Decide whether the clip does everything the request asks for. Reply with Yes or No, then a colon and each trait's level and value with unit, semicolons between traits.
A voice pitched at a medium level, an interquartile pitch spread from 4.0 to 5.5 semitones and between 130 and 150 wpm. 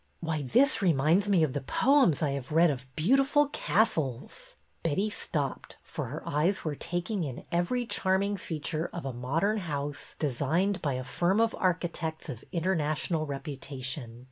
No: medium, 160 Hz; average, 5.2 semitones; average, 160 wpm